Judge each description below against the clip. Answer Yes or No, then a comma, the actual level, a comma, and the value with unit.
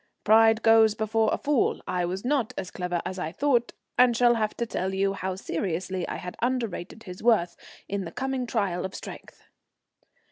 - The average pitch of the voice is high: Yes, high, 215 Hz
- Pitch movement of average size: Yes, average, 4.2 semitones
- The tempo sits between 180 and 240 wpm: Yes, average, 185 wpm